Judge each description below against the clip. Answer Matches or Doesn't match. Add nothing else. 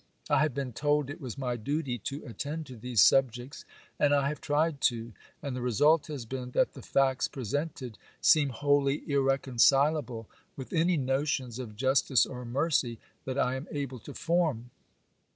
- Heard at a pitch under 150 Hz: Matches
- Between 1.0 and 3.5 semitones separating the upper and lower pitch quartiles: Matches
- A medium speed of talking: Matches